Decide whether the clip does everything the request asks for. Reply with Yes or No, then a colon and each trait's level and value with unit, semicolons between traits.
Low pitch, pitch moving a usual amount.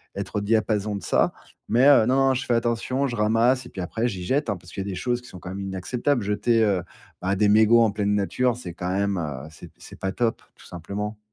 Yes: low, 105 Hz; average, 3.7 semitones